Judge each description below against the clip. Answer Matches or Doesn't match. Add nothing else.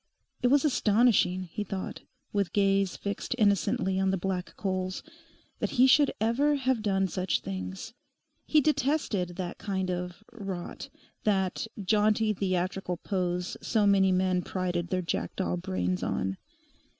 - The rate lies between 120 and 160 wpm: Matches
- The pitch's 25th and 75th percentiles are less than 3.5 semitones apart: Matches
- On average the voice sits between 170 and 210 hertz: Matches